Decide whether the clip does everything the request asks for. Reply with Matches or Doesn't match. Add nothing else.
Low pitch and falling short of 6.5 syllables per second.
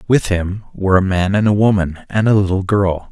Matches